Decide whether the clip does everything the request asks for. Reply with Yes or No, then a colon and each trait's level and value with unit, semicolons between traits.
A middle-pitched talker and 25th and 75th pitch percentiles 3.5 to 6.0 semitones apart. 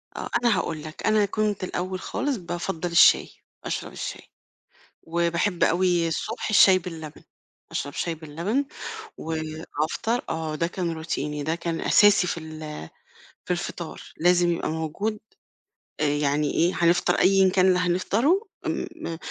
No: medium, 170 Hz; average, 3.1 semitones